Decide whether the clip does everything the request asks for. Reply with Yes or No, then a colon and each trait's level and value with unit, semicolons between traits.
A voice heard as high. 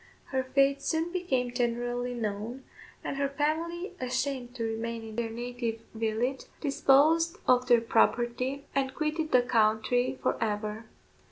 Yes: very high, 250 Hz